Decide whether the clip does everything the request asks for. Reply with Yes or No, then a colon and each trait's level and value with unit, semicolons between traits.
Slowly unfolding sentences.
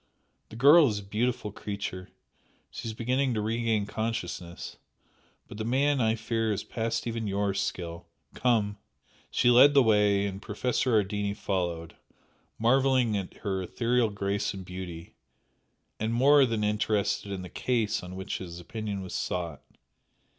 No: average, 150 wpm